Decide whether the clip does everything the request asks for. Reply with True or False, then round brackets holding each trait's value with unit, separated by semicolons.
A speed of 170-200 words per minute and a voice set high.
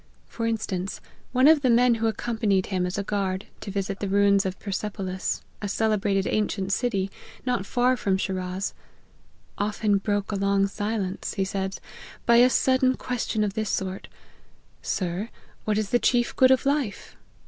True (180 wpm; 205 Hz)